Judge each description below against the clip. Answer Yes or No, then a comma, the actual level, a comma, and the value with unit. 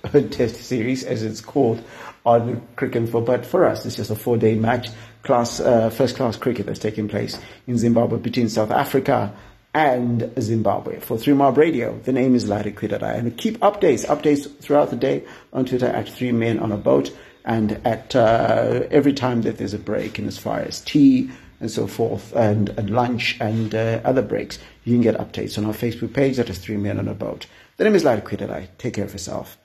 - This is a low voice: Yes, low, 115 Hz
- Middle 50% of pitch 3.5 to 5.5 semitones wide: No, narrow, 2.6 semitones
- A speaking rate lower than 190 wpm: No, fast, 205 wpm